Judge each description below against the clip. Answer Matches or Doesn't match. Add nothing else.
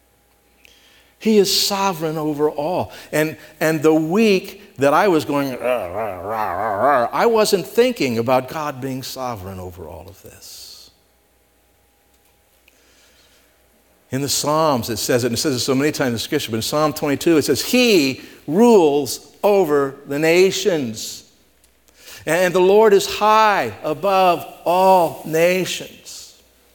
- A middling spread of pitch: Doesn't match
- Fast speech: Doesn't match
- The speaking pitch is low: Doesn't match